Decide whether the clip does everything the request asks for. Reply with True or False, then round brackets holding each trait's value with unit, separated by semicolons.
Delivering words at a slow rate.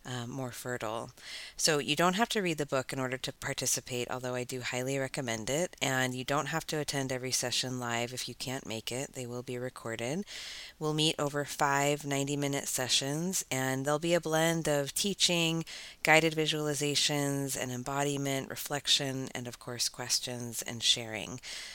False (175 wpm)